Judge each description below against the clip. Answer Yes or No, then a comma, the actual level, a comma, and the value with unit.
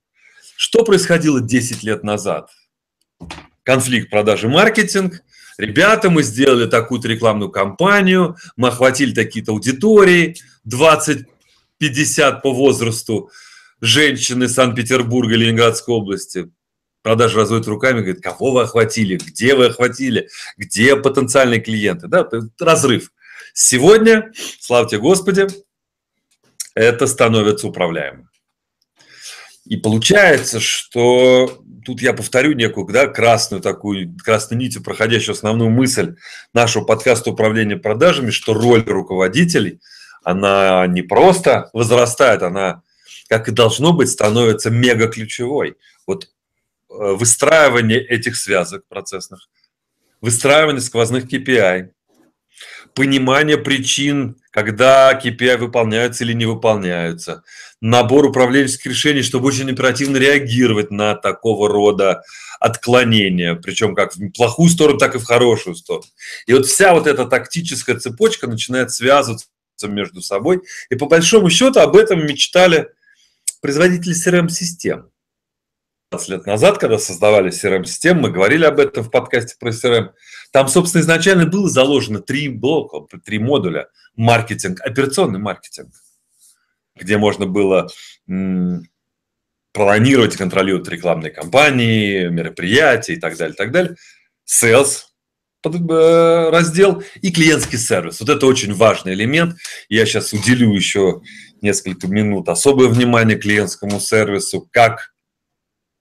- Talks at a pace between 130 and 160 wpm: No, average, 115 wpm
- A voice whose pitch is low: Yes, low, 120 Hz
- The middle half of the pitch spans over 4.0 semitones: Yes, average, 5.2 semitones